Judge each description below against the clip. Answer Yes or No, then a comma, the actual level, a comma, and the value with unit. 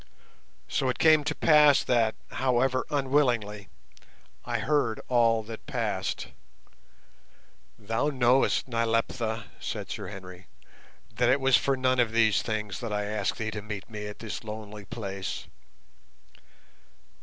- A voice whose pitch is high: No, low, 115 Hz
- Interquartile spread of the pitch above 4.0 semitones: No, average, 3.3 semitones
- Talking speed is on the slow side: Yes, slow, 130 wpm